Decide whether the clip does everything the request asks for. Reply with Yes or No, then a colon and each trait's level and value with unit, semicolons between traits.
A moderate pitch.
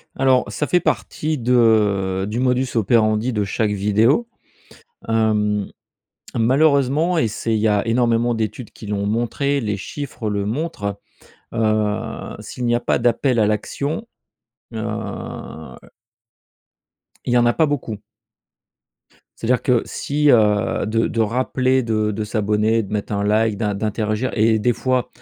No: low, 115 Hz